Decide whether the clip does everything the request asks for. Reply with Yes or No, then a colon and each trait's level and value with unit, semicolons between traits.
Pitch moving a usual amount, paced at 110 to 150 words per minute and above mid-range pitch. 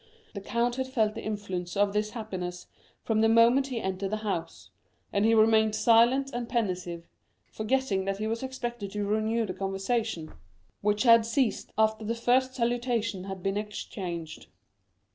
No: average, 3.1 semitones; average, 160 wpm; high, 215 Hz